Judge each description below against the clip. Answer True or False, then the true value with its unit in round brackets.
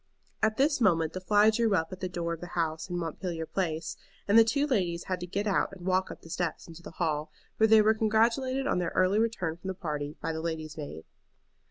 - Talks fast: True (240 wpm)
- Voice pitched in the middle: True (180 Hz)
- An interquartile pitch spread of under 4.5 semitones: False (4.8 semitones)